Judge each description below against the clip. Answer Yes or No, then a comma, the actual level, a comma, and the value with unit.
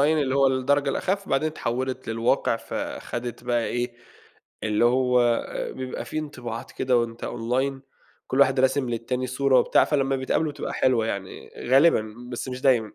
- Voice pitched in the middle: No, low, 130 Hz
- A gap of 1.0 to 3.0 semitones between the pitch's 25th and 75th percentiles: Yes, narrow, 2.4 semitones